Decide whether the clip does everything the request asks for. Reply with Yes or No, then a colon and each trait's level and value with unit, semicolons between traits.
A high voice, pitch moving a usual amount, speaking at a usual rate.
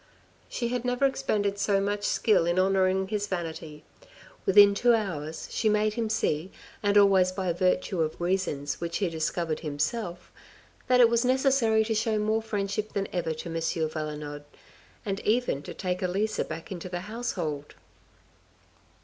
Yes: high, 195 Hz; average, 4.4 semitones; average, 160 wpm